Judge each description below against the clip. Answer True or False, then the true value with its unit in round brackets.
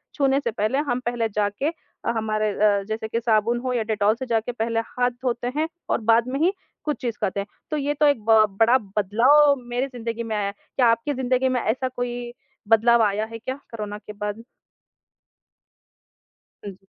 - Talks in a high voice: True (230 Hz)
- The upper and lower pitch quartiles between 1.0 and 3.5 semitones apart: True (2.9 semitones)